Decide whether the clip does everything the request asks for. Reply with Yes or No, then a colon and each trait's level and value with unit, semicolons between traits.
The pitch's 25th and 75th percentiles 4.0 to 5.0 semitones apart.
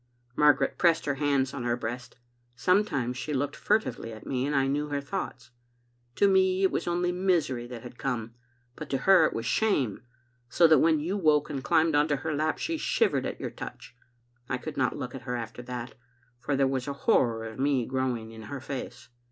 Yes: average, 4.3 semitones